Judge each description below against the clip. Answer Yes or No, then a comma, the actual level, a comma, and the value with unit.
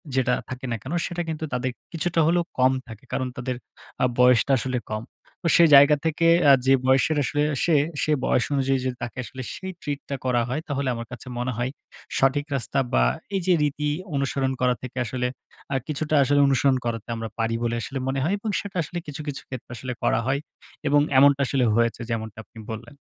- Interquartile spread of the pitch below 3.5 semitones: Yes, average, 2.9 semitones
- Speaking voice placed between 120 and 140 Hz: Yes, low, 135 Hz